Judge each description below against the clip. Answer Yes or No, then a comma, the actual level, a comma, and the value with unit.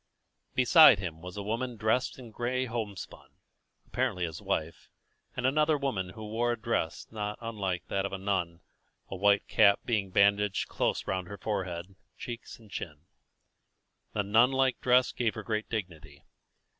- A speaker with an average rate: Yes, average, 160 wpm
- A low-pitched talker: Yes, low, 105 Hz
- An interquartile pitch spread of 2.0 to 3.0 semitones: No, average, 4.1 semitones